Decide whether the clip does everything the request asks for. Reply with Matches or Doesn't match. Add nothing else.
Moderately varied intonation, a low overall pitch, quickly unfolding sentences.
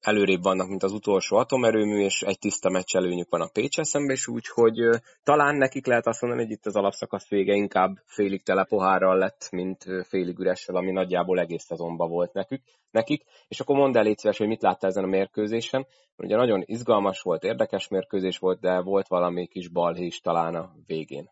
Matches